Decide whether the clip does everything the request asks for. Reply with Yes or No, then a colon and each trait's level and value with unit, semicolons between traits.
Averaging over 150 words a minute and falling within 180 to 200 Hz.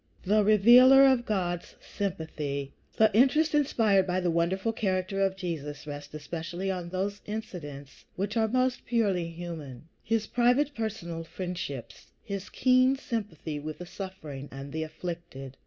No: average, 145 wpm; medium, 185 Hz